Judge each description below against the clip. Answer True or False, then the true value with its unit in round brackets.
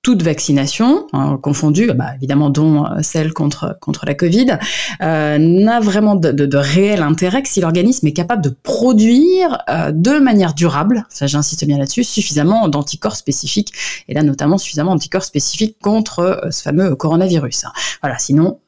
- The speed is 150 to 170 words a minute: True (160 wpm)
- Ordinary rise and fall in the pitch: False (5.9 semitones)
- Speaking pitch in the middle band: True (165 Hz)